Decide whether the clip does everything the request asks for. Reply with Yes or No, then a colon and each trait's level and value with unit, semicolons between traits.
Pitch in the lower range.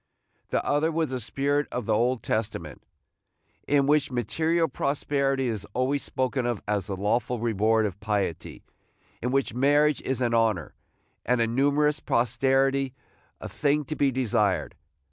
Yes: low, 130 Hz